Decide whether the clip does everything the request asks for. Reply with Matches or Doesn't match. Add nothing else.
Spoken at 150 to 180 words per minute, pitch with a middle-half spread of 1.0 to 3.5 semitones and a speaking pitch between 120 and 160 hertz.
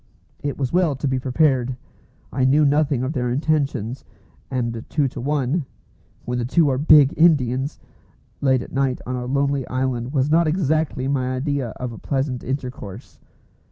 Matches